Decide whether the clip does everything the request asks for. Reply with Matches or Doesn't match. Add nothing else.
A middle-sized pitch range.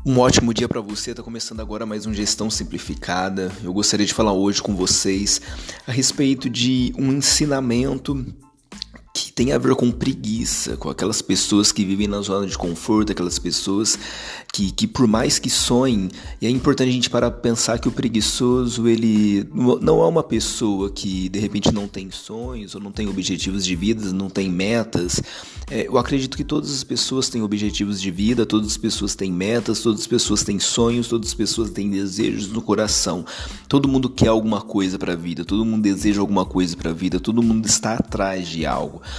Matches